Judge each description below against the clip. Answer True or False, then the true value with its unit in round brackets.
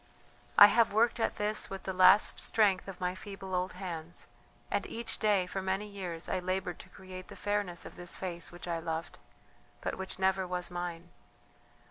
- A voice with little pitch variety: True (2.1 semitones)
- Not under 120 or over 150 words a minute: False (185 wpm)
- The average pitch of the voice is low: False (185 Hz)